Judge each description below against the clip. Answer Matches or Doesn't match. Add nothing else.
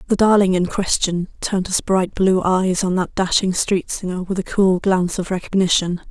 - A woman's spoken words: Matches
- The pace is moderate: Matches